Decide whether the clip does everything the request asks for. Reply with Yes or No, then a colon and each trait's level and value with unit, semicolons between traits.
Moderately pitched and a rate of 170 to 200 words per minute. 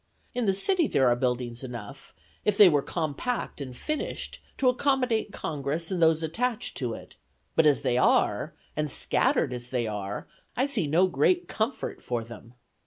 Yes: medium, 150 Hz; average, 175 wpm